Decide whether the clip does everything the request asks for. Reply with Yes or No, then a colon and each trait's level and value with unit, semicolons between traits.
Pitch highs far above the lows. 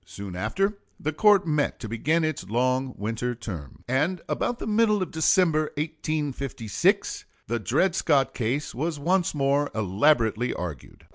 Yes: wide, 6.0 semitones